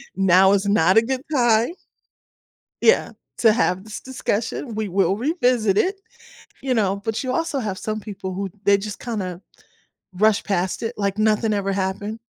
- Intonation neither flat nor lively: Yes, average, 3.2 semitones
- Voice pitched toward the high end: Yes, high, 210 Hz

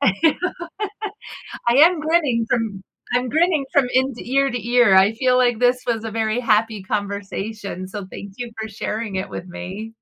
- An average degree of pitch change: Yes, average, 3.7 semitones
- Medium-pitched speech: No, high, 225 Hz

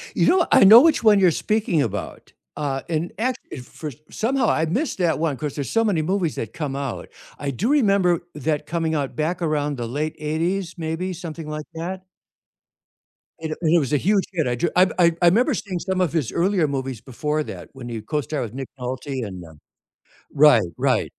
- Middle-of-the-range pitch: Yes, medium, 160 Hz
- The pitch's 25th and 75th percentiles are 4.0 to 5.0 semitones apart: Yes, average, 4.6 semitones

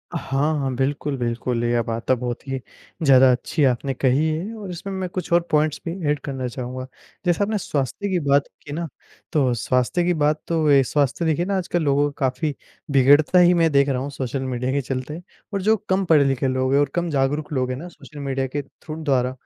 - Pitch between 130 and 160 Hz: Yes, medium, 140 Hz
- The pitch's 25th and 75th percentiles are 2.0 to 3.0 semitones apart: No, average, 4.0 semitones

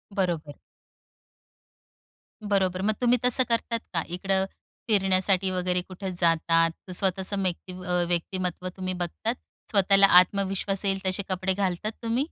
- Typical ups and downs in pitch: No, narrow, 1.6 semitones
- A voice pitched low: No, high, 190 Hz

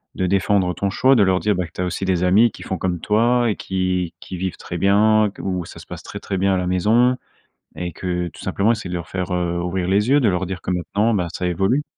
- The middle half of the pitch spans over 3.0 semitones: No, average, 2.7 semitones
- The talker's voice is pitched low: Yes, very low, 95 Hz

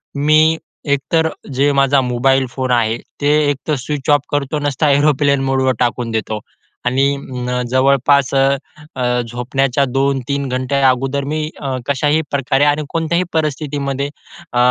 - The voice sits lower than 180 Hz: Yes, low, 135 Hz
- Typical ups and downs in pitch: No, narrow, 2.1 semitones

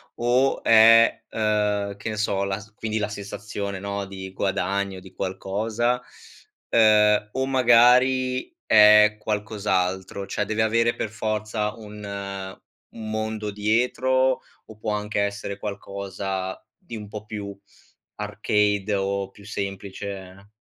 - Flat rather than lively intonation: Yes, narrow, 1.8 semitones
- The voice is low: Yes, low, 105 Hz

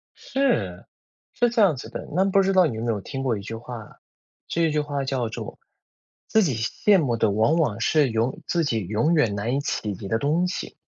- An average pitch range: No, wide, 7.0 semitones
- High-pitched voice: No, low, 135 Hz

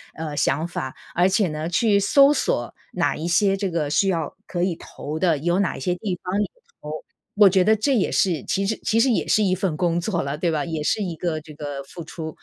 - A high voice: No, medium, 175 Hz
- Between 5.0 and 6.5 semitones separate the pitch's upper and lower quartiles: No, average, 4.0 semitones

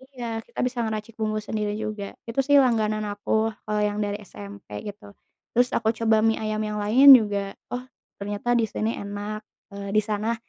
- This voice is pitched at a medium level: No, high, 215 Hz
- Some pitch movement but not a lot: No, narrow, 1.7 semitones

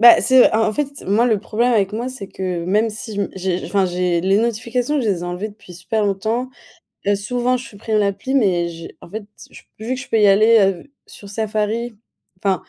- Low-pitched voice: No, high, 210 Hz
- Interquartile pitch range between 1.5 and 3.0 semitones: No, average, 3.4 semitones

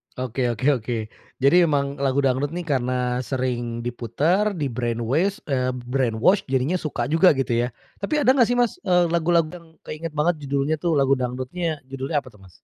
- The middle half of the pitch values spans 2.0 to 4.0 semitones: No, average, 4.9 semitones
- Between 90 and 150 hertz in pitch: Yes, medium, 140 Hz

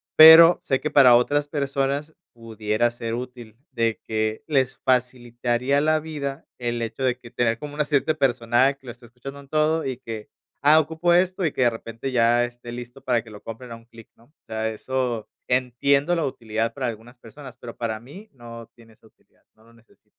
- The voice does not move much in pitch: No, average, 3.3 semitones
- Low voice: Yes, low, 125 Hz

